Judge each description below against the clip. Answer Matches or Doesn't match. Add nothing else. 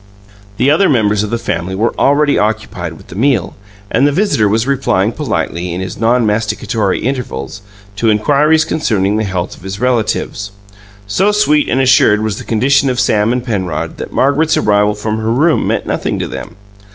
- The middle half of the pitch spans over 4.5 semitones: Matches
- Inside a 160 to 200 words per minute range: Matches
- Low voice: Matches